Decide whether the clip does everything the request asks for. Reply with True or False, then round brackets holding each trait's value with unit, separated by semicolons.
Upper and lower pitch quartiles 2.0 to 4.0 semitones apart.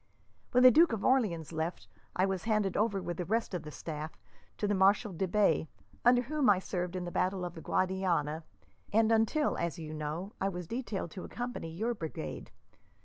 False (4.8 semitones)